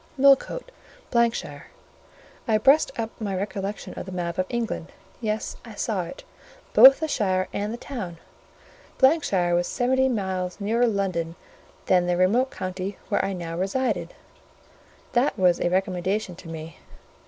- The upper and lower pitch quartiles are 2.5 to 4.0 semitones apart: No, average, 4.8 semitones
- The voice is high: Yes, high, 195 Hz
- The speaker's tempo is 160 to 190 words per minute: No, average, 145 wpm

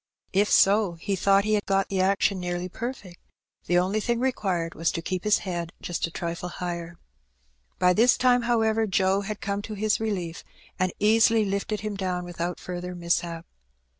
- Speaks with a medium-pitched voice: No, high, 195 Hz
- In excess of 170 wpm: Yes, average, 180 wpm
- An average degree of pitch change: Yes, average, 3.2 semitones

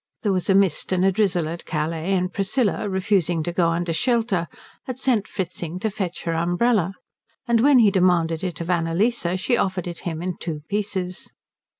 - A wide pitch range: No, average, 3.3 semitones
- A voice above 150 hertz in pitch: Yes, medium, 185 Hz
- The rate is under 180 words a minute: No, average, 190 wpm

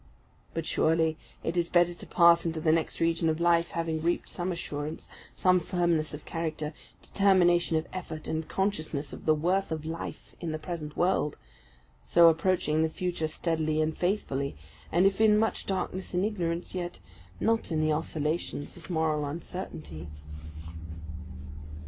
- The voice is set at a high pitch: No, medium, 165 Hz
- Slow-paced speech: No, average, 155 wpm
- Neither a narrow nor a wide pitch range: No, narrow, 2.1 semitones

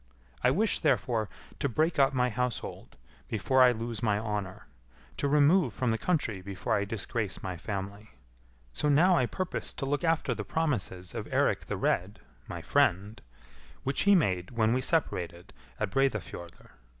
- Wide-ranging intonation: Yes, wide, 6.0 semitones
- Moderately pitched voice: No, low, 115 Hz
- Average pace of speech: Yes, average, 160 wpm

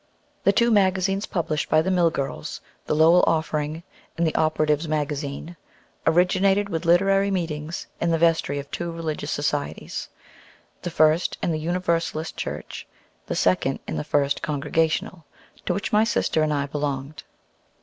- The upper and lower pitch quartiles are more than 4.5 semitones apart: No, average, 2.9 semitones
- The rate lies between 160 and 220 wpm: No, average, 150 wpm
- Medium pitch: Yes, medium, 160 Hz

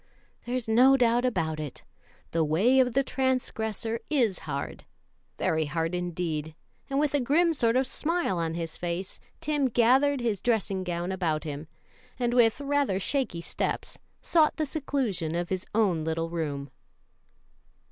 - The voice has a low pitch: No, high, 220 Hz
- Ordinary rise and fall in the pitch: No, wide, 7.7 semitones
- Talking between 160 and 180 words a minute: No, average, 150 wpm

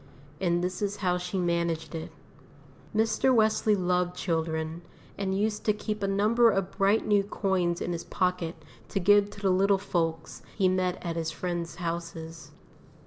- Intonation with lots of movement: No, average, 2.9 semitones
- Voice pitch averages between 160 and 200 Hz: Yes, medium, 185 Hz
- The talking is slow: No, average, 165 wpm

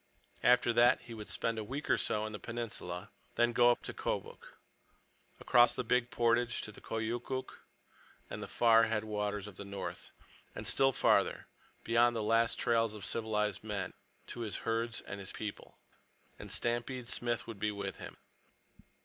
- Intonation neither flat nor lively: No, narrow, 2.1 semitones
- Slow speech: No, average, 165 wpm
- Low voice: Yes, low, 115 Hz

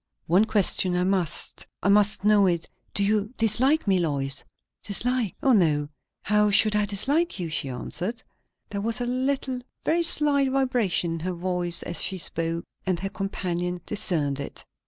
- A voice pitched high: Yes, high, 200 Hz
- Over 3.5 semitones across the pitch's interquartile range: Yes, average, 4.7 semitones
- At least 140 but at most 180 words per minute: Yes, average, 165 wpm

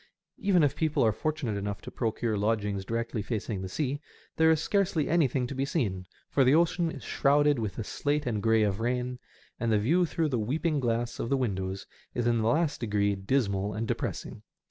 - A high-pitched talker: No, low, 120 Hz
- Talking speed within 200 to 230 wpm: Yes, fast, 205 wpm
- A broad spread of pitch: Yes, wide, 5.8 semitones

